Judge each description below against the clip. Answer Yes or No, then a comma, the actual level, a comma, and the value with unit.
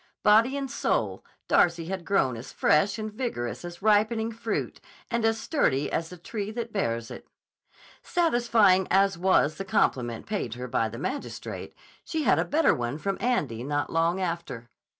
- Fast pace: No, average, 170 wpm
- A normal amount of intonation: No, wide, 7.6 semitones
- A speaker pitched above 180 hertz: Yes, high, 190 Hz